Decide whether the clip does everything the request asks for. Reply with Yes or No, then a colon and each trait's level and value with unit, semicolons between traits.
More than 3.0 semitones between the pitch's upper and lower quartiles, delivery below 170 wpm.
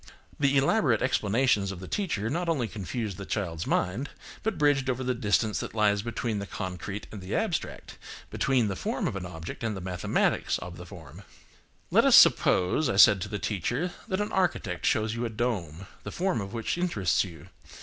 No: average, 5.3 semitones; average, 195 wpm